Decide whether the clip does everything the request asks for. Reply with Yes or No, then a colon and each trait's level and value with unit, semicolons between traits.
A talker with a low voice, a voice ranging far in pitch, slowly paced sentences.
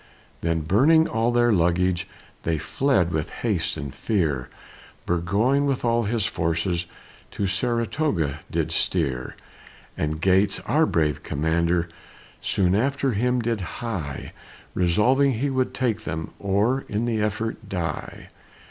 Yes: low, 100 Hz; wide, 6.1 semitones; slow, 130 wpm